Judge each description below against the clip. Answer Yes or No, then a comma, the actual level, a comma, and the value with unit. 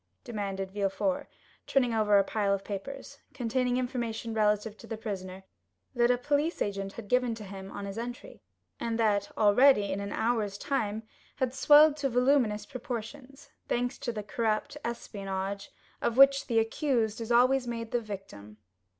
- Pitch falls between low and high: No, high, 225 Hz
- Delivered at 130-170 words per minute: Yes, average, 160 wpm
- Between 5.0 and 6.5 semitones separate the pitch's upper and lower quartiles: No, average, 3.7 semitones